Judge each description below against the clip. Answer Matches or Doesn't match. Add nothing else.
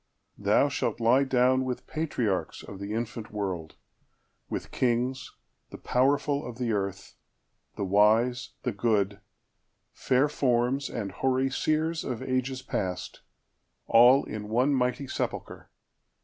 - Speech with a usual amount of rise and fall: Matches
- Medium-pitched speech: Doesn't match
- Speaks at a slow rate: Matches